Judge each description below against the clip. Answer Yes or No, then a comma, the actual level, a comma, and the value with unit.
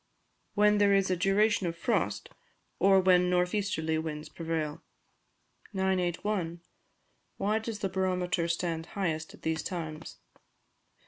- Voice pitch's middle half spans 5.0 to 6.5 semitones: No, average, 3.1 semitones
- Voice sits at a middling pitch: Yes, medium, 180 Hz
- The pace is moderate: No, slow, 130 wpm